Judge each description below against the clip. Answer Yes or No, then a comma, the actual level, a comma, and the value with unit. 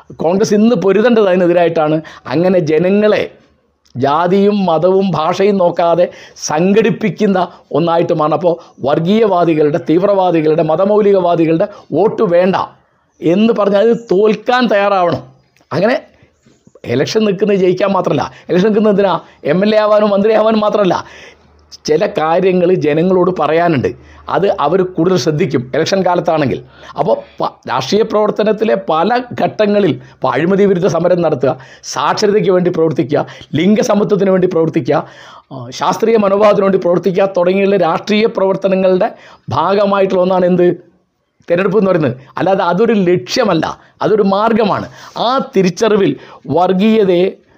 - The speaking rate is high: No, average, 105 wpm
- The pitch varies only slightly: No, average, 3.8 semitones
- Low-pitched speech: No, medium, 185 Hz